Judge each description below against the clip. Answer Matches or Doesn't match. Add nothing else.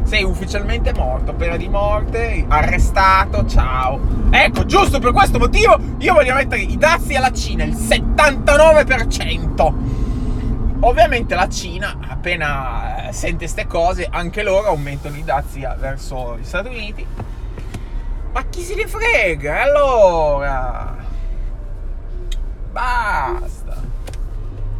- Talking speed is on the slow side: Matches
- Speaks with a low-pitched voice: Matches